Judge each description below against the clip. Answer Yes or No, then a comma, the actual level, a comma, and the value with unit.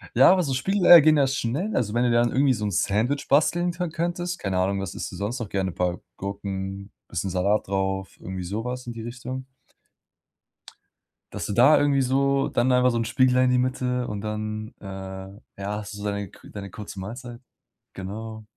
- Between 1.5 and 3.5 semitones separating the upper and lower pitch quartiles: No, average, 4.8 semitones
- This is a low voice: Yes, low, 115 Hz